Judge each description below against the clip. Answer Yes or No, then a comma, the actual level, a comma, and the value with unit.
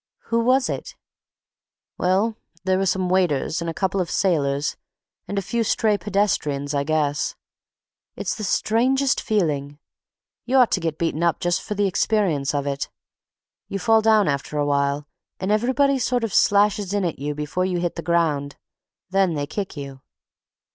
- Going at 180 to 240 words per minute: No, average, 170 wpm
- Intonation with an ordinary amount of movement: No, wide, 6.1 semitones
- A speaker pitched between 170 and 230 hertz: Yes, medium, 185 Hz